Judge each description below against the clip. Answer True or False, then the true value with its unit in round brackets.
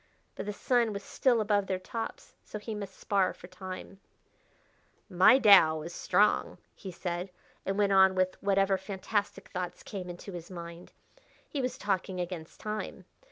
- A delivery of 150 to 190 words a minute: True (160 wpm)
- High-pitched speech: True (195 Hz)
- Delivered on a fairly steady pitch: True (2.3 semitones)